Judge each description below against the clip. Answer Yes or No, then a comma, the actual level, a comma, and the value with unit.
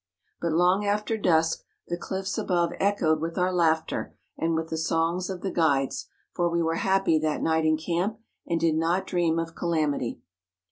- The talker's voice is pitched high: No, medium, 170 Hz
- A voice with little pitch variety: Yes, narrow, 2.1 semitones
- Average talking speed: Yes, average, 180 wpm